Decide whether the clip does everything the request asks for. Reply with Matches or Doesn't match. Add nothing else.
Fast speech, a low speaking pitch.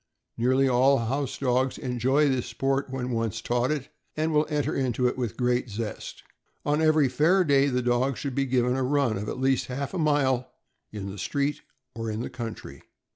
Doesn't match